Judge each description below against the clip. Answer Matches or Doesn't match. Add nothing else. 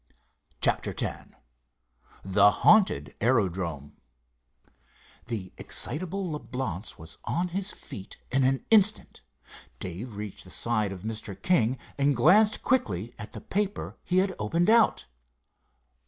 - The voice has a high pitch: Doesn't match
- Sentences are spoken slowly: Matches